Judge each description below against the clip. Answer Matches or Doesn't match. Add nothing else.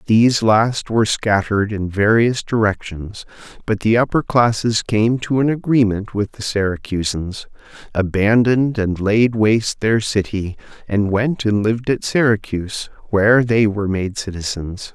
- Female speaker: Doesn't match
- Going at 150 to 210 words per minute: Doesn't match